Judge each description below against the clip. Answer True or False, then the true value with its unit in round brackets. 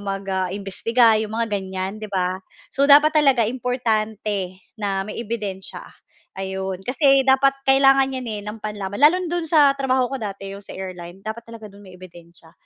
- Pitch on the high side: True (215 Hz)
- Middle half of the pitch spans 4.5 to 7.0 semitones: True (5.5 semitones)